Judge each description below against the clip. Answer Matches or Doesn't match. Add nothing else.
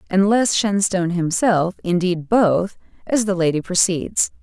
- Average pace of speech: Doesn't match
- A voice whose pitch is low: Doesn't match